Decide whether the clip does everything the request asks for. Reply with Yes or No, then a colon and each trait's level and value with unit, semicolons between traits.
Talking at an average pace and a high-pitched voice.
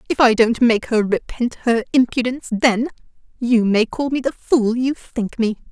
Yes: average, 190 wpm; high, 235 Hz